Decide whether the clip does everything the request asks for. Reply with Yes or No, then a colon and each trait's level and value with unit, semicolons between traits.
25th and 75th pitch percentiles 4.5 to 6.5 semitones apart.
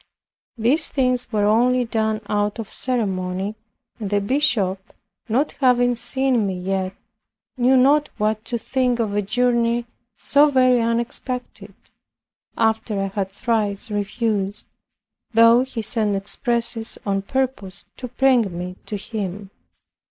No: average, 3.7 semitones